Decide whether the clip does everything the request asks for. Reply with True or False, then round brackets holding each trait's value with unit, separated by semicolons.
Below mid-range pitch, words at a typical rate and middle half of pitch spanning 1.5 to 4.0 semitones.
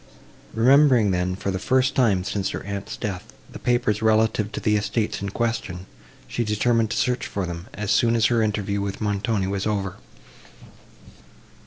True (105 Hz; 170 wpm; 2.7 semitones)